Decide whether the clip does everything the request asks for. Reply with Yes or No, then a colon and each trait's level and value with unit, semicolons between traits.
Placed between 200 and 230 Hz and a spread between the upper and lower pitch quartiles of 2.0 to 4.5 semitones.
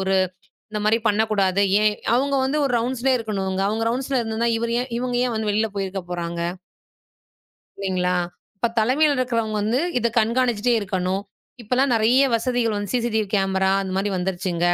Yes: high, 220 Hz; average, 4.0 semitones